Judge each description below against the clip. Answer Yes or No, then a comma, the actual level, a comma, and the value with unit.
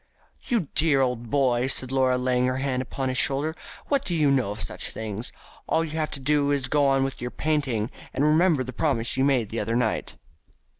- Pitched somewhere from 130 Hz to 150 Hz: Yes, low, 135 Hz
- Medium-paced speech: No, fast, 230 wpm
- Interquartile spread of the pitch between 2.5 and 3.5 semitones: Yes, average, 3.0 semitones